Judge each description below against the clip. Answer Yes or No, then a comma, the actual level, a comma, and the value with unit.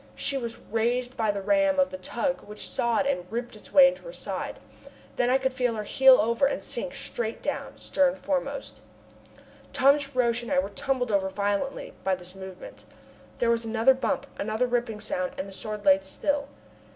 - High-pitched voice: Yes, high, 240 Hz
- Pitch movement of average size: Yes, average, 4.5 semitones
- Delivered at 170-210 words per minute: Yes, average, 190 wpm